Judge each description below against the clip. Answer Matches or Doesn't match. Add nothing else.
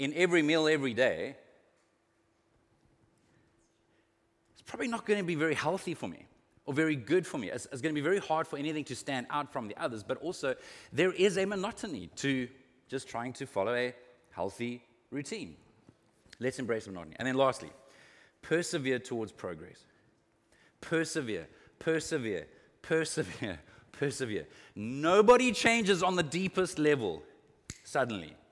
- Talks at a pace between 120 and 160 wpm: Matches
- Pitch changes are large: Matches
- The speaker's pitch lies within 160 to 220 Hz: Doesn't match